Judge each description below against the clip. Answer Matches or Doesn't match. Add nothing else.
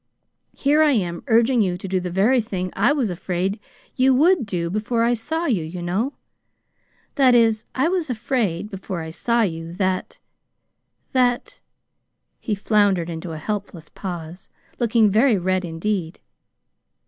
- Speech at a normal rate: Matches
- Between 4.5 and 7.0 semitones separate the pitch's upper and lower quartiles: Matches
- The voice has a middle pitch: Doesn't match